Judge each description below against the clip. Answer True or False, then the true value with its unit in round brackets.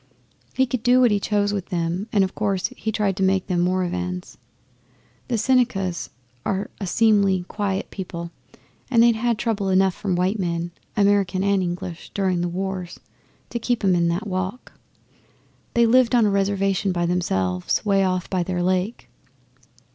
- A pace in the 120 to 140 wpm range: False (170 wpm)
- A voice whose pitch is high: True (195 Hz)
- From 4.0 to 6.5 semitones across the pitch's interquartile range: False (2.7 semitones)